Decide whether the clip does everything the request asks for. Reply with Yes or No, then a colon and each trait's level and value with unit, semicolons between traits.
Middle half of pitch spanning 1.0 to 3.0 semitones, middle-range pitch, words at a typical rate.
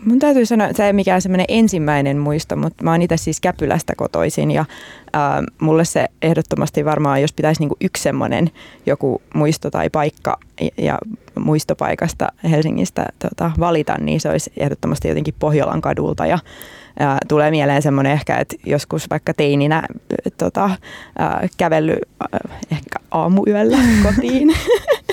No: average, 5.3 semitones; medium, 160 Hz; average, 145 wpm